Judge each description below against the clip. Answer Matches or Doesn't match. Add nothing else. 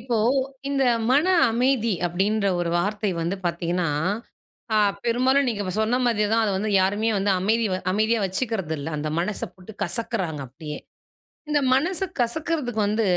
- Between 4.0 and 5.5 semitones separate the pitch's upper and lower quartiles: Matches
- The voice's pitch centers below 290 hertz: Matches